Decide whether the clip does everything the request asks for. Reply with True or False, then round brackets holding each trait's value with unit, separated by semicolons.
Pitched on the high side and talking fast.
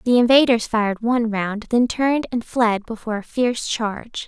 False (230 Hz; 185 wpm)